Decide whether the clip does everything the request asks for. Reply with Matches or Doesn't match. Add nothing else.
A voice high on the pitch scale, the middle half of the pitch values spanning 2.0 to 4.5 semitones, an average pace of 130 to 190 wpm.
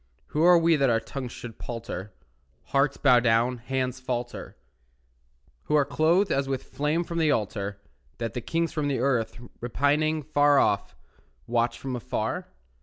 Doesn't match